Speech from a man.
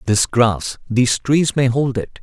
Yes: male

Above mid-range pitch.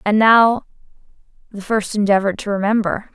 Yes: high, 210 Hz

